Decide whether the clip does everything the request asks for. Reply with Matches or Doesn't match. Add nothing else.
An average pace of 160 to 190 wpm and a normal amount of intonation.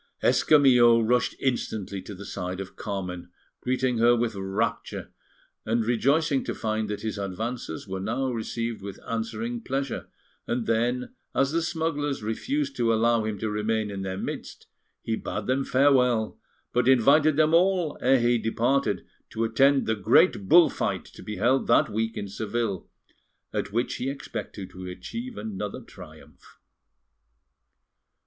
Doesn't match